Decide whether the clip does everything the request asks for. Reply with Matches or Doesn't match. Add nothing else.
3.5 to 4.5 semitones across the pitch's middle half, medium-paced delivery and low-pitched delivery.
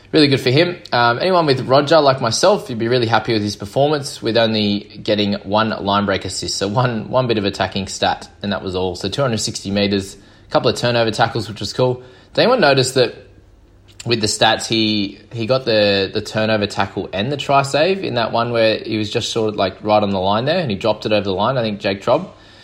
Doesn't match